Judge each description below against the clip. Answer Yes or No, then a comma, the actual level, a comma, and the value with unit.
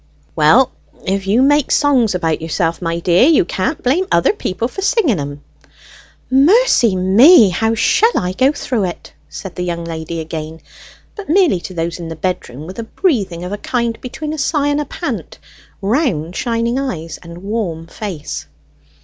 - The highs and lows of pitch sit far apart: Yes, wide, 8.1 semitones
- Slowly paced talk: No, average, 175 wpm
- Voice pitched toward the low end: No, high, 195 Hz